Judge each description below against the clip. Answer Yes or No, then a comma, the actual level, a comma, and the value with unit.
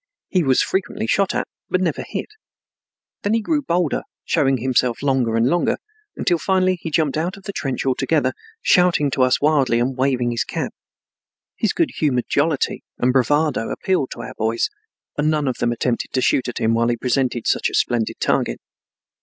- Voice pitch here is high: No, low, 135 Hz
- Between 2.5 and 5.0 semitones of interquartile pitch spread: No, wide, 5.4 semitones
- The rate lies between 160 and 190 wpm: Yes, average, 185 wpm